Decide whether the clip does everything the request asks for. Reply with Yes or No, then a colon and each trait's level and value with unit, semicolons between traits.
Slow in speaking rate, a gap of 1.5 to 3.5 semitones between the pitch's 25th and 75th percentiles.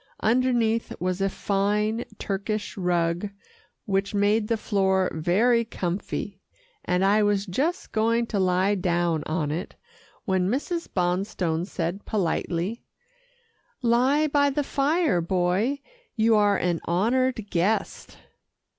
No: slow, 120 wpm; average, 4.2 semitones